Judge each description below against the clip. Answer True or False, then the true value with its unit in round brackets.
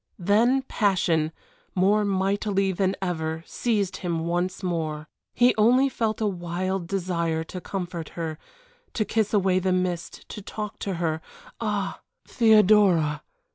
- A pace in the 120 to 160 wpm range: True (135 wpm)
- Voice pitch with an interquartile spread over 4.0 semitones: False (3.5 semitones)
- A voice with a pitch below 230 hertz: True (190 Hz)